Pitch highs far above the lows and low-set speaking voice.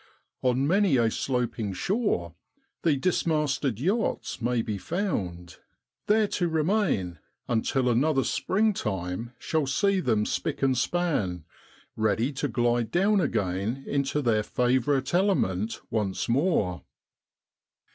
Yes: wide, 7.4 semitones; low, 130 Hz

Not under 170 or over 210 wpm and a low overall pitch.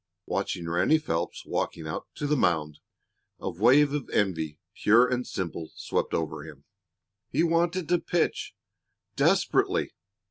No: slow, 135 wpm; low, 105 Hz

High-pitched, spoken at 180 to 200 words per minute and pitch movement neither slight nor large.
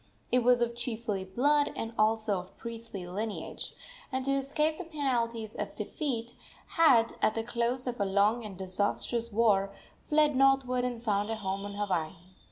No: high, 230 Hz; average, 170 wpm; average, 3.7 semitones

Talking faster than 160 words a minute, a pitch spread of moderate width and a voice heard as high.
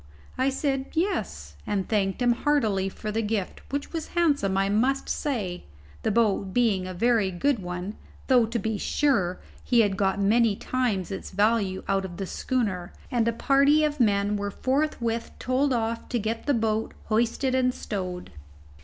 Yes: average, 170 wpm; average, 4.6 semitones; high, 225 Hz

